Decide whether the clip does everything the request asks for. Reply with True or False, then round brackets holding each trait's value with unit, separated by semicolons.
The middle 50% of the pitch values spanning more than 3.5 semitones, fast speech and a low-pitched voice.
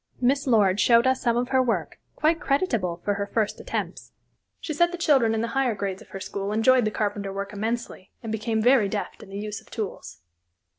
False (4.1 semitones; 215 wpm; 220 Hz)